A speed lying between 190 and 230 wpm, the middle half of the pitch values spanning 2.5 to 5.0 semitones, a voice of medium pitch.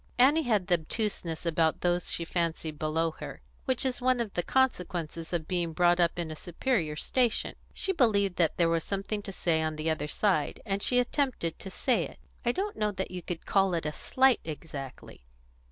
No: average, 200 wpm; wide, 5.6 semitones; medium, 180 Hz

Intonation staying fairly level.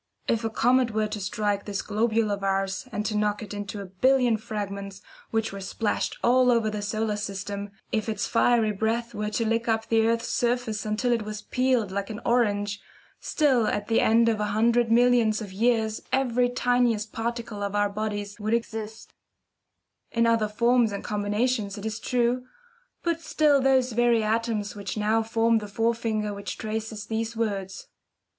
Yes: narrow, 2.2 semitones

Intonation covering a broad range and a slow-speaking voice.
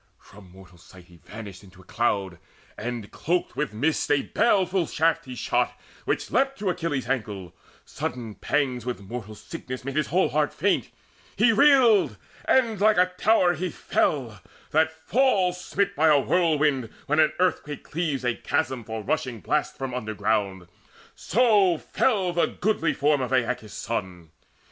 No: wide, 8.3 semitones; average, 155 wpm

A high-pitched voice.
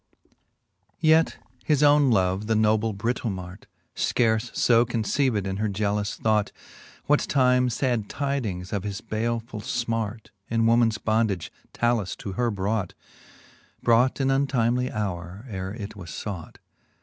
No: low, 110 Hz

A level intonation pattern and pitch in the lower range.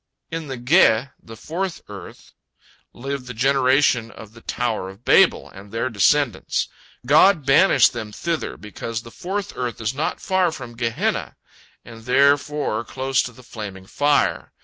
No: average, 4.3 semitones; low, 125 Hz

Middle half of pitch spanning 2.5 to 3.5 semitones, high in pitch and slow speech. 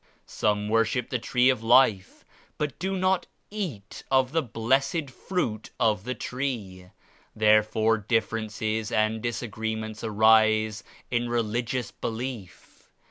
No: average, 2.8 semitones; low, 115 Hz; slow, 115 wpm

